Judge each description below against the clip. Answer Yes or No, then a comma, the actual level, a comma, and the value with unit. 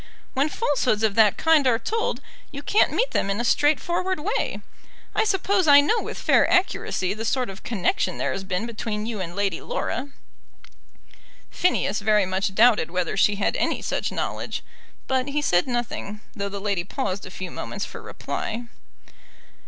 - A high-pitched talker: Yes, high, 225 Hz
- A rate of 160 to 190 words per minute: Yes, average, 175 wpm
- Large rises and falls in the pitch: Yes, wide, 6.6 semitones